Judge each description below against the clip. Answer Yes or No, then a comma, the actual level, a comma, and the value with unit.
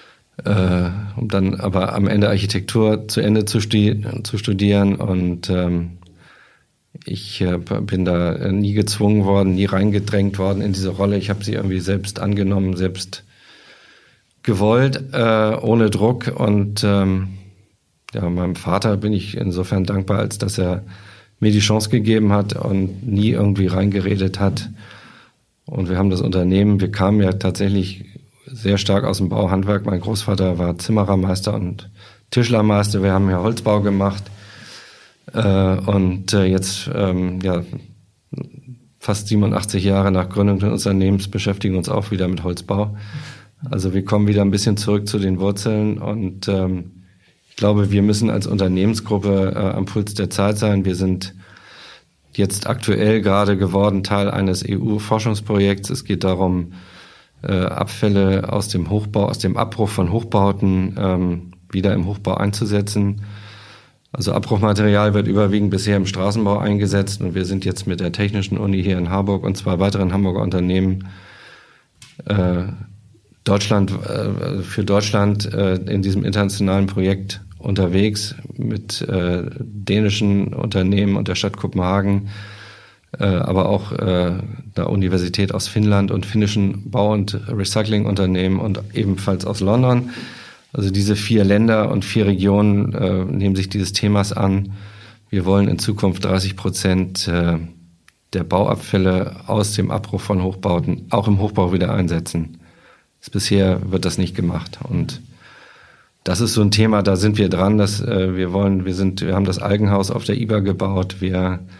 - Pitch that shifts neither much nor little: No, narrow, 1.7 semitones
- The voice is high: No, low, 100 Hz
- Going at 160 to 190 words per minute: No, average, 145 wpm